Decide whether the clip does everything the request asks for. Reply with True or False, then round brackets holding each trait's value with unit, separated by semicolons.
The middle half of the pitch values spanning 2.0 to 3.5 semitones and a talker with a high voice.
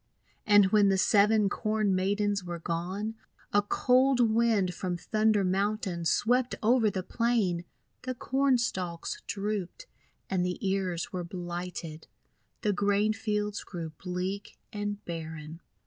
True (3.2 semitones; 200 Hz)